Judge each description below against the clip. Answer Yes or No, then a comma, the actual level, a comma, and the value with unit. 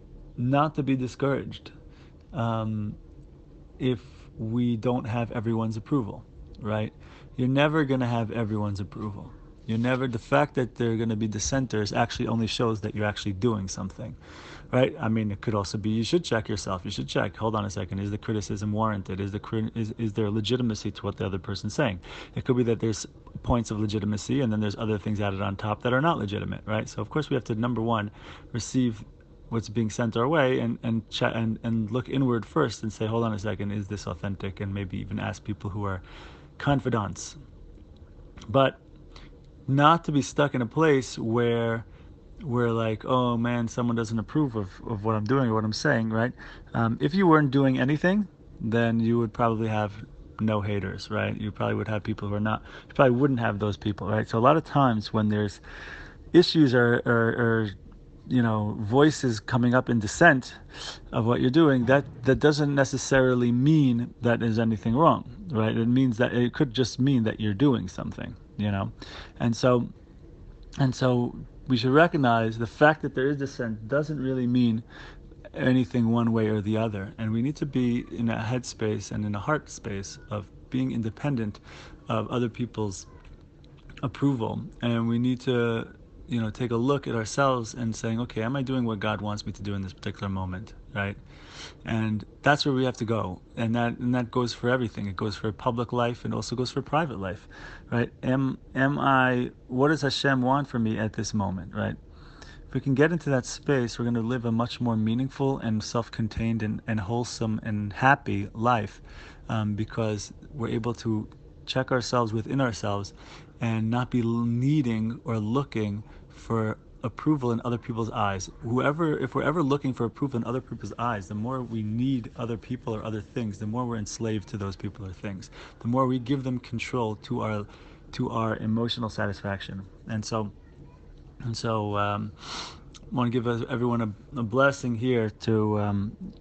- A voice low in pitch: Yes, low, 115 Hz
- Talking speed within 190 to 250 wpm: Yes, average, 200 wpm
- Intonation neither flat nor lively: Yes, average, 3.1 semitones